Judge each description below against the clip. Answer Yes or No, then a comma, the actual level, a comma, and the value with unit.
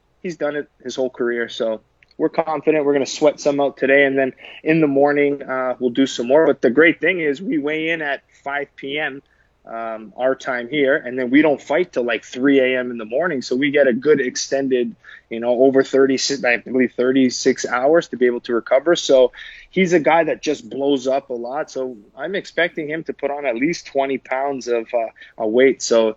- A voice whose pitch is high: No, low, 135 Hz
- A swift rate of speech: Yes, fast, 220 wpm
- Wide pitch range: No, average, 2.9 semitones